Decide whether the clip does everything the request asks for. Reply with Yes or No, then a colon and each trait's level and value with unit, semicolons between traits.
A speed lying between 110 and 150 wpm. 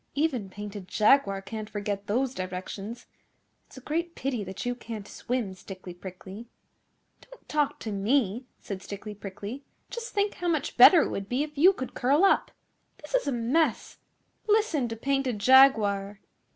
No: average, 165 wpm